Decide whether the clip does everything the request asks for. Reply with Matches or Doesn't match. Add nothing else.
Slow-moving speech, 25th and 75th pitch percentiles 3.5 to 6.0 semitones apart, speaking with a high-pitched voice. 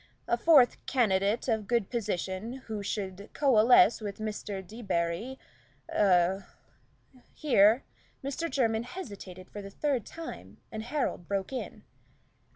Matches